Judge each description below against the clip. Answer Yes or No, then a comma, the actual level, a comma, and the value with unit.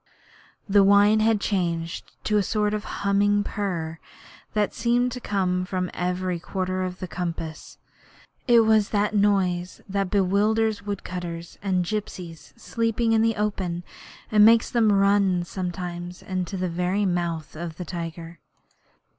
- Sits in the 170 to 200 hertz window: Yes, high, 190 Hz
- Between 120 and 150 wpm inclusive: Yes, average, 140 wpm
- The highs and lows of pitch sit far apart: No, average, 2.9 semitones